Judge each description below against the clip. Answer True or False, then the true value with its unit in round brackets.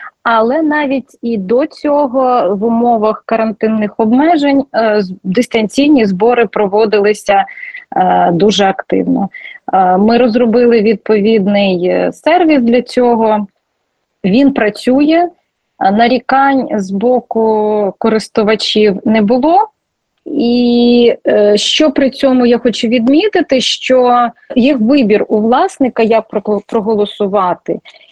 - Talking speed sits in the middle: False (90 wpm)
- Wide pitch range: False (4.0 semitones)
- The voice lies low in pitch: False (235 Hz)